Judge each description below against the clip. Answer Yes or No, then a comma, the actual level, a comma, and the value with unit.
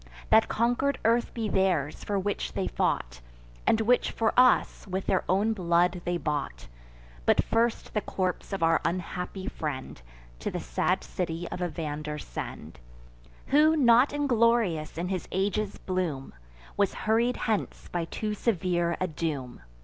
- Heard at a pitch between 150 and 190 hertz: Yes, medium, 185 Hz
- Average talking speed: Yes, average, 150 wpm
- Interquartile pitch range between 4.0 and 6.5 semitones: Yes, average, 5.2 semitones